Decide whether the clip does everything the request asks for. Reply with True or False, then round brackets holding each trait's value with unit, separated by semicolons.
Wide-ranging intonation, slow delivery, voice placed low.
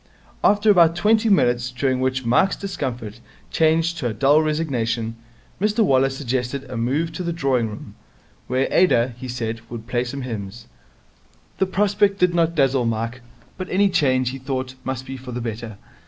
False (5.7 semitones; 170 wpm; 130 Hz)